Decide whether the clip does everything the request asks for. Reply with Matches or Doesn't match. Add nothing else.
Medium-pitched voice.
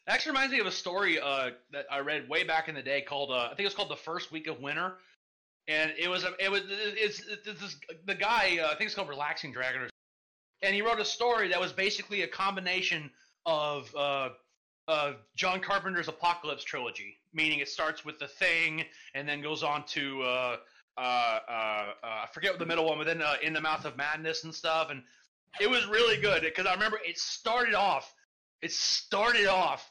Matches